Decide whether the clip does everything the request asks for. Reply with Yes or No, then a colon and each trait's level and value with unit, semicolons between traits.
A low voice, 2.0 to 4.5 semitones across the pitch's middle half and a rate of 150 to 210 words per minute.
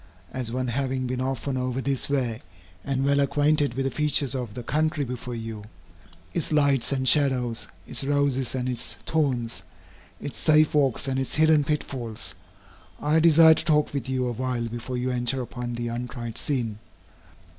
Yes: low, 130 Hz; average, 2.7 semitones; average, 170 wpm